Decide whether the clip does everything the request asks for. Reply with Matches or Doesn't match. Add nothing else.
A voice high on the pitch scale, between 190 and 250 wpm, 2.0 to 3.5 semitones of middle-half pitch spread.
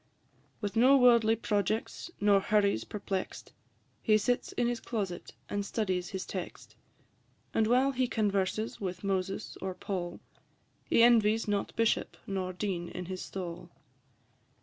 Doesn't match